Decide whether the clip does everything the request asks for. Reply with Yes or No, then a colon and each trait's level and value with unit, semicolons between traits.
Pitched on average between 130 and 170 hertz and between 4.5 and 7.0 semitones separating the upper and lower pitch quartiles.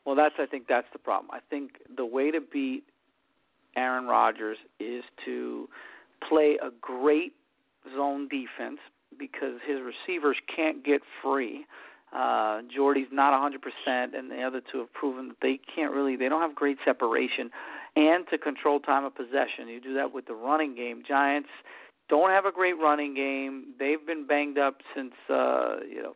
No: medium, 140 Hz; narrow, 2.5 semitones